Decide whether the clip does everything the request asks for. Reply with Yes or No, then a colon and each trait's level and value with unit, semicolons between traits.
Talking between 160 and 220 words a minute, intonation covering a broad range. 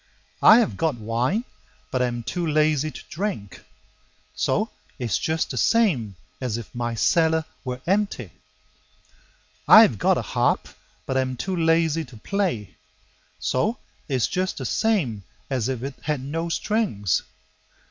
No: average, 145 wpm; wide, 6.4 semitones